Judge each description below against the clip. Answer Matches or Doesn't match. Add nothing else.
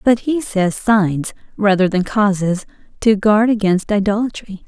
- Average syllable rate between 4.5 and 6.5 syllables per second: Doesn't match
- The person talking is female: Matches